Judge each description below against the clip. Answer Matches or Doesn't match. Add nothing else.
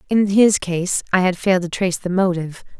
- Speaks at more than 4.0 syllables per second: Matches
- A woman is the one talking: Matches